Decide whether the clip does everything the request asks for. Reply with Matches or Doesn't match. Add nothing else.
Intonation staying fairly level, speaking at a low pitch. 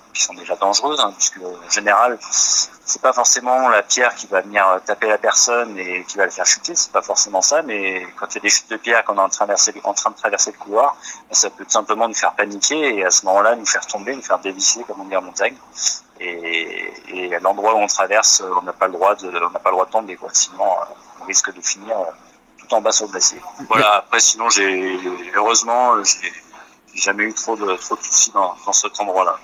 Doesn't match